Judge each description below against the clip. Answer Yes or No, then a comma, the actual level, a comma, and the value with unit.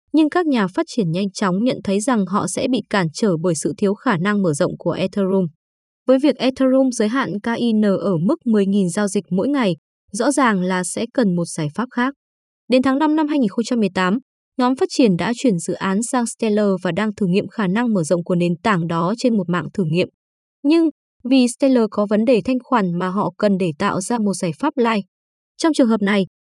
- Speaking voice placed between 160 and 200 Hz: No, high, 210 Hz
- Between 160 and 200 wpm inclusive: No, average, 225 wpm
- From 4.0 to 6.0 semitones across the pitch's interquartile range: Yes, average, 5.1 semitones